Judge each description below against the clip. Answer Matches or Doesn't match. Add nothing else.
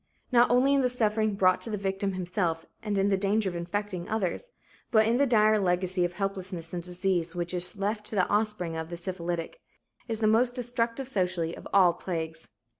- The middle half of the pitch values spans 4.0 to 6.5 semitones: Doesn't match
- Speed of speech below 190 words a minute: Doesn't match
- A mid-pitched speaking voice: Doesn't match